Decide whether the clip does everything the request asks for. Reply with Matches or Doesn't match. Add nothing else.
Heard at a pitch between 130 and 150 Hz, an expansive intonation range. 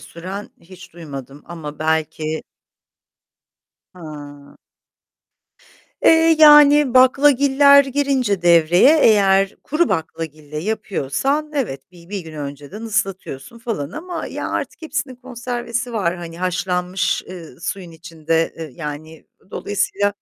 Doesn't match